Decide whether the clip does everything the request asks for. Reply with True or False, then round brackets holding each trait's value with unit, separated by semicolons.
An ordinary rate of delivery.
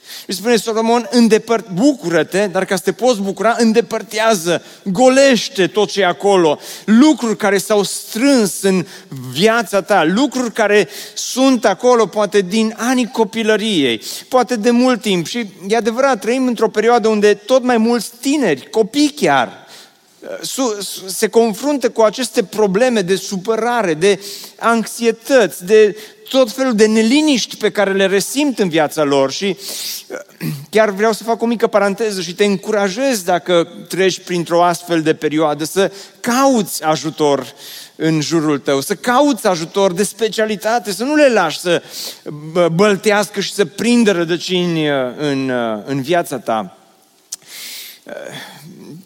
True (135 wpm)